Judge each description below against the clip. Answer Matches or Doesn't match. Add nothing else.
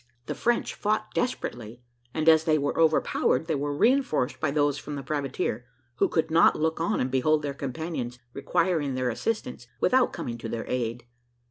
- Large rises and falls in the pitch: Doesn't match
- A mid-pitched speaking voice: Matches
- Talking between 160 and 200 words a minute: Matches